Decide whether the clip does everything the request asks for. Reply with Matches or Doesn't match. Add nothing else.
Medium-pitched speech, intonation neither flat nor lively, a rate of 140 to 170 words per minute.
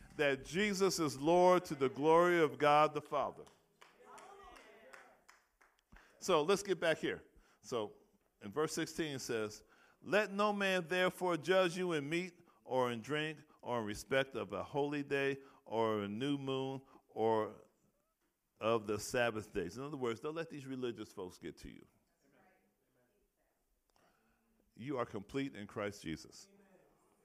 Doesn't match